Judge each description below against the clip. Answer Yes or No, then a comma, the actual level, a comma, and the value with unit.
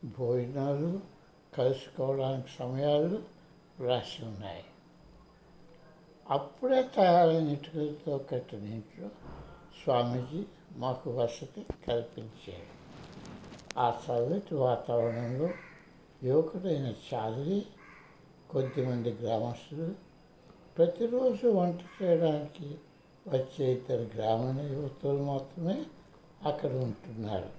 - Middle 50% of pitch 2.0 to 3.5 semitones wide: No, average, 5.2 semitones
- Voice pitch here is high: No, medium, 140 Hz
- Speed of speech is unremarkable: No, slow, 65 wpm